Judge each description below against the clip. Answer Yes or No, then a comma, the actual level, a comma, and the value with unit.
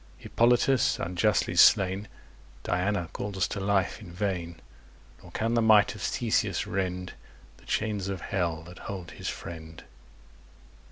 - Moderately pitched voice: No, very low, 95 Hz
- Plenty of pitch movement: No, average, 2.8 semitones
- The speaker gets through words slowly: Yes, slow, 130 wpm